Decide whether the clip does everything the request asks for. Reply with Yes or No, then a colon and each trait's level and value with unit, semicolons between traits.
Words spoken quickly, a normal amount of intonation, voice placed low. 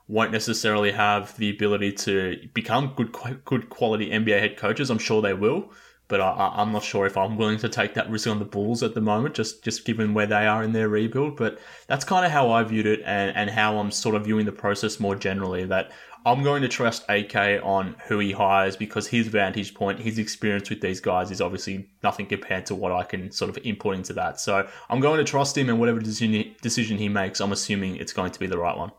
No: fast, 240 wpm; narrow, 2.0 semitones; low, 105 Hz